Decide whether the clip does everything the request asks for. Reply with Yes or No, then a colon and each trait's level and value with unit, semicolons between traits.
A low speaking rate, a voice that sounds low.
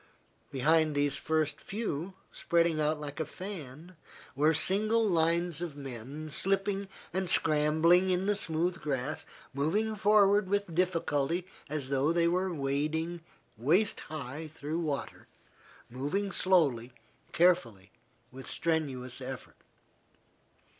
No: slow, 115 wpm; medium, 160 Hz